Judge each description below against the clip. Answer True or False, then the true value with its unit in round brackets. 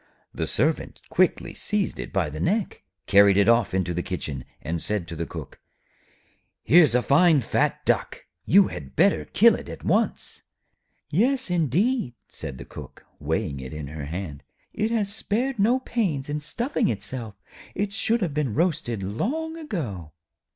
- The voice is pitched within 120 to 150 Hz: True (140 Hz)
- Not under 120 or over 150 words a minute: False (165 wpm)